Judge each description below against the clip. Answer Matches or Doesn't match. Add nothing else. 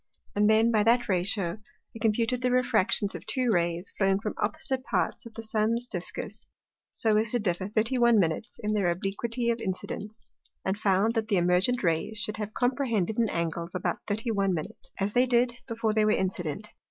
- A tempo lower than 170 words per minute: Doesn't match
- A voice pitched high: Matches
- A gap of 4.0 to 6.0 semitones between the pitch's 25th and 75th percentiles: Doesn't match